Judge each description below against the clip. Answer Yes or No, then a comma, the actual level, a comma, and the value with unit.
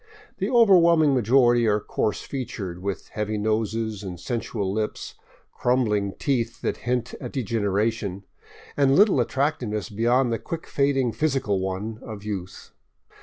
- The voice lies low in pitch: Yes, low, 115 Hz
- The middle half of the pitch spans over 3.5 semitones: Yes, average, 4.2 semitones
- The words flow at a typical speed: No, slow, 130 wpm